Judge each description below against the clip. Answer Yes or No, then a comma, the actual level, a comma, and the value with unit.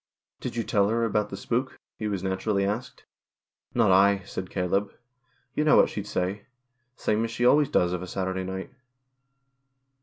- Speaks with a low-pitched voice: Yes, low, 100 Hz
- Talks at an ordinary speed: Yes, average, 185 wpm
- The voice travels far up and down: No, average, 3.2 semitones